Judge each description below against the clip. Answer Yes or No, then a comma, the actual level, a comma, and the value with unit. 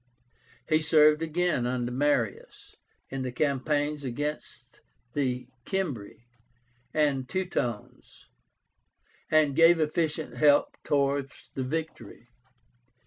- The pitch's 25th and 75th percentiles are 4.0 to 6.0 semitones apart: No, average, 3.4 semitones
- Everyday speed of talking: No, slow, 90 wpm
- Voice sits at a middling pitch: Yes, medium, 145 Hz